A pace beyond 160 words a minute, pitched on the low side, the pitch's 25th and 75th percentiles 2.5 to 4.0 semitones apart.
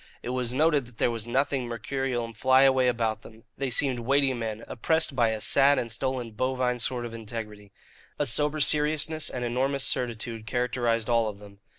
Yes: average, 185 wpm; low, 125 Hz; average, 2.8 semitones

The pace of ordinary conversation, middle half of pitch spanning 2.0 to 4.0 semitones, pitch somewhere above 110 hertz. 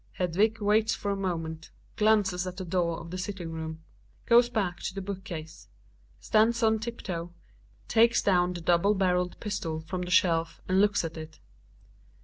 Yes: average, 180 wpm; average, 3.7 semitones; medium, 185 Hz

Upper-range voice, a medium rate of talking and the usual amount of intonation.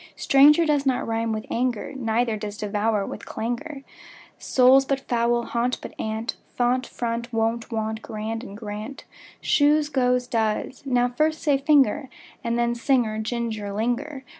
Yes: high, 240 Hz; average, 155 wpm; average, 3.2 semitones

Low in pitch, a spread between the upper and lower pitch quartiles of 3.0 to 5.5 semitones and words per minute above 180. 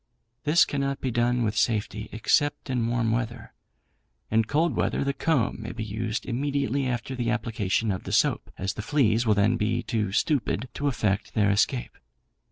No: low, 115 Hz; average, 3.6 semitones; average, 175 wpm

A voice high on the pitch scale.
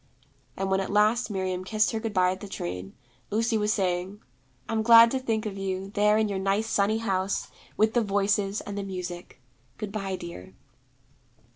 Yes: high, 200 Hz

